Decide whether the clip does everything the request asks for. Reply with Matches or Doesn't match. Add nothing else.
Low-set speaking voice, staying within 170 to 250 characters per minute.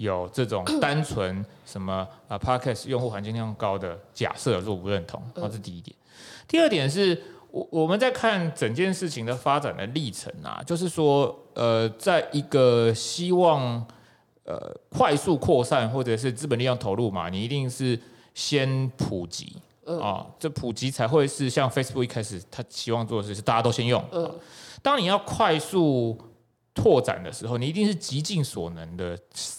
Doesn't match